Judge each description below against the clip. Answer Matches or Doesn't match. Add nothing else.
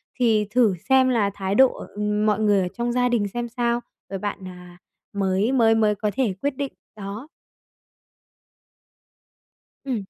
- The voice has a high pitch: Matches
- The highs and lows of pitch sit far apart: Doesn't match